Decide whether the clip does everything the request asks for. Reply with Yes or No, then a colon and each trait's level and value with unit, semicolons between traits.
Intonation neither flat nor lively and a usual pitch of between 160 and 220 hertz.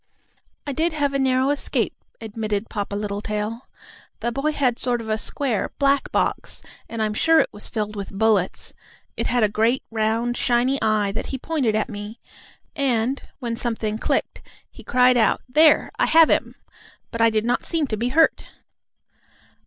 No: average, 3.8 semitones; high, 235 Hz